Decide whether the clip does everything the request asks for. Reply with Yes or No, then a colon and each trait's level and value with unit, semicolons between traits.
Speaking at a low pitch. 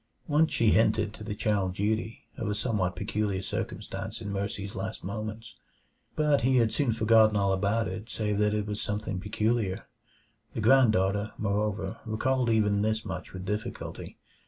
Yes: low, 105 Hz